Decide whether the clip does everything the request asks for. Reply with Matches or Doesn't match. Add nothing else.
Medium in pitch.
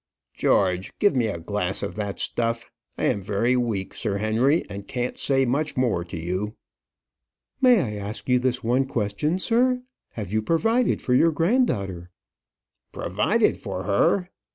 Doesn't match